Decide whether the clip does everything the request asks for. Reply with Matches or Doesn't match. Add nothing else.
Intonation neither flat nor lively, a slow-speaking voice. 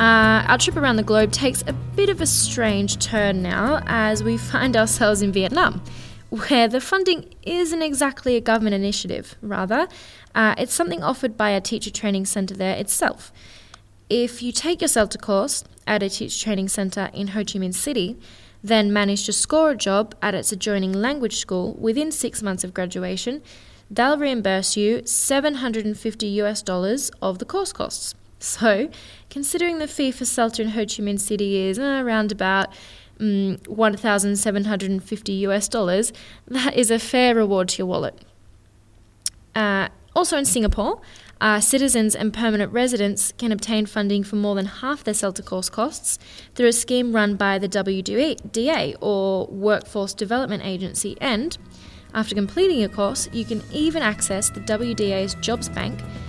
Doesn't match